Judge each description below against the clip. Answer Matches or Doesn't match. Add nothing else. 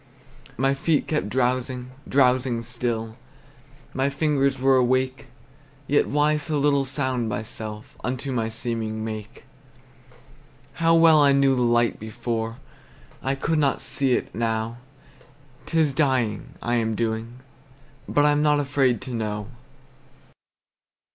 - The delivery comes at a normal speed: Doesn't match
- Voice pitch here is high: Doesn't match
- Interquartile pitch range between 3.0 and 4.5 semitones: Matches